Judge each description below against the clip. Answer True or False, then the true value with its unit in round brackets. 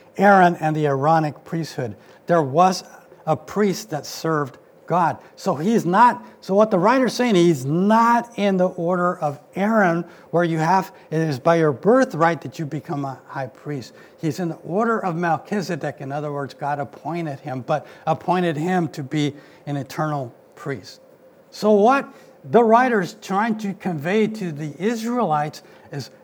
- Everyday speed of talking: True (165 wpm)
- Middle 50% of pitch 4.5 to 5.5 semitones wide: True (5.0 semitones)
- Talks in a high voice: False (170 Hz)